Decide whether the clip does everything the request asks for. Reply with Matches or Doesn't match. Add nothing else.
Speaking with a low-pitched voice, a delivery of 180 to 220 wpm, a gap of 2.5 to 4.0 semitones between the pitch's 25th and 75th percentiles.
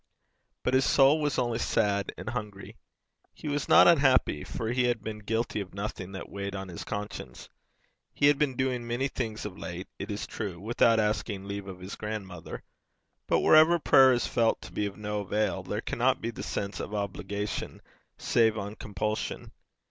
Matches